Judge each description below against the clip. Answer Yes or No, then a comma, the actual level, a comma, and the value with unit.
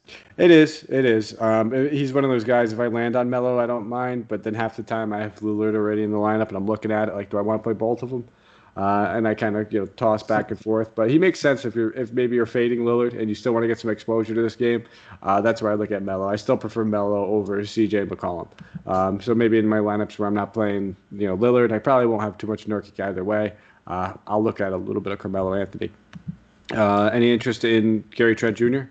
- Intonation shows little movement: Yes, narrow, 2.3 semitones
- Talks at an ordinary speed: No, fast, 270 wpm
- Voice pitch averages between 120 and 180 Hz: No, low, 110 Hz